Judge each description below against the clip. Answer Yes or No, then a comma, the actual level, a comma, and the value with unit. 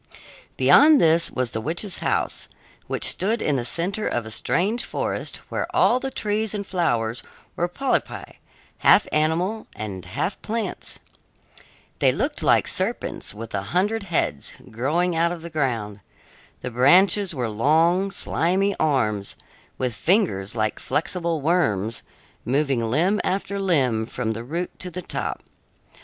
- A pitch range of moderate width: No, wide, 8.3 semitones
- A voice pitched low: No, medium, 160 Hz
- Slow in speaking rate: No, average, 145 wpm